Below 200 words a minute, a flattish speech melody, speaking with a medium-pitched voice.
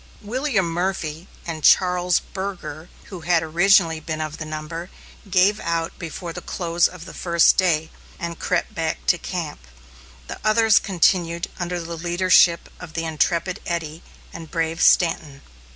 Yes: average, 150 wpm; narrow, 1.9 semitones; medium, 170 Hz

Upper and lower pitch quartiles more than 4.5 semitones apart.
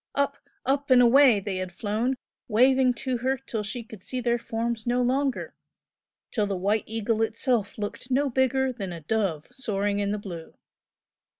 No: average, 4.0 semitones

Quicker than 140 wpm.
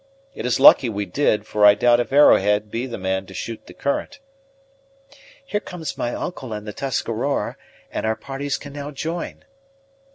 Yes: average, 175 wpm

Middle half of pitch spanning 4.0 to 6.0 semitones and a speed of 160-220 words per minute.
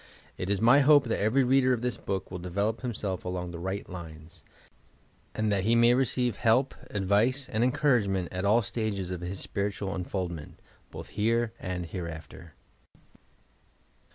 Yes: average, 4.4 semitones; average, 165 wpm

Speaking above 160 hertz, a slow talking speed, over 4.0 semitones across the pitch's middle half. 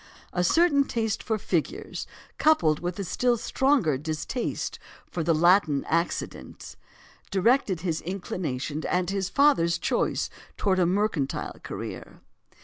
Yes: medium, 185 Hz; slow, 125 wpm; average, 5.3 semitones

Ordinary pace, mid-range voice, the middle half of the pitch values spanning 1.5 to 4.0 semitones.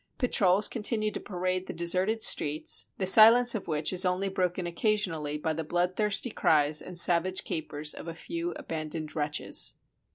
No: average, 160 wpm; medium, 180 Hz; average, 4.8 semitones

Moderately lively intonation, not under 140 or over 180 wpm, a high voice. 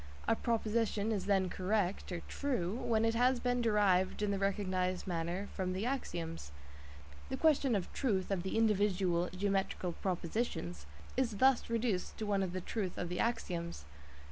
Yes: average, 3.8 semitones; average, 160 wpm; high, 200 Hz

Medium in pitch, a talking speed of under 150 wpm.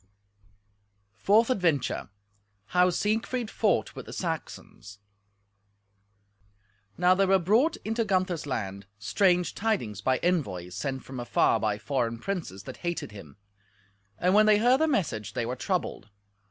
Yes: medium, 175 Hz; slow, 135 wpm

